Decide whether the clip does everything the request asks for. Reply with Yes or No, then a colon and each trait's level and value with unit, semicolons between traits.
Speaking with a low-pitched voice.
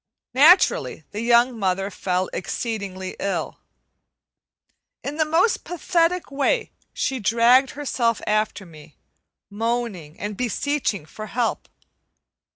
No: high, 230 Hz